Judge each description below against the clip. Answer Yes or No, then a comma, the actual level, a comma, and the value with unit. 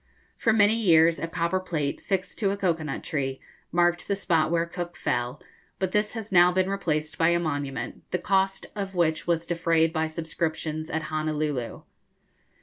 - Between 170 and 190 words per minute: Yes, average, 175 wpm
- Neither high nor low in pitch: Yes, medium, 170 Hz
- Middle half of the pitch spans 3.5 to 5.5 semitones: No, average, 3.1 semitones